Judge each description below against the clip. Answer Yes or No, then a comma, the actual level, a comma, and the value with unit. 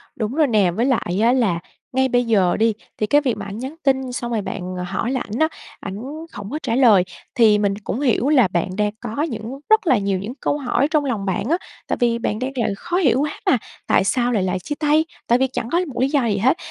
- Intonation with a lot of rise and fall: No, average, 4.7 semitones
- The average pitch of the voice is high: Yes, high, 240 Hz